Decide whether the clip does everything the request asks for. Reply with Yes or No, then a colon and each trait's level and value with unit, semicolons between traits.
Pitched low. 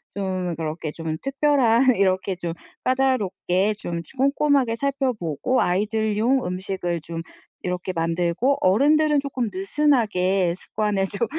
No: high, 200 Hz